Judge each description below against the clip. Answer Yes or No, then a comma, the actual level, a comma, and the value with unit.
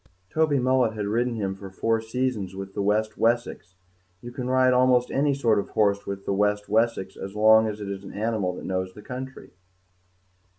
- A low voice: Yes, low, 110 Hz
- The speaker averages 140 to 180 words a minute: No, average, 200 wpm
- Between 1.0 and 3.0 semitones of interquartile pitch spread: No, average, 3.9 semitones